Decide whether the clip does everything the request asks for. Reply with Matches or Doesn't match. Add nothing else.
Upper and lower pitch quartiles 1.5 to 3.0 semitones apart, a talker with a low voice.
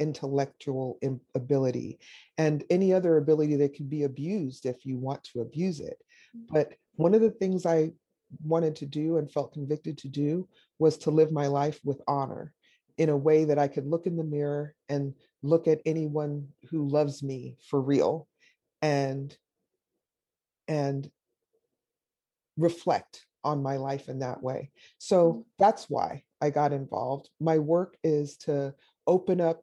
Doesn't match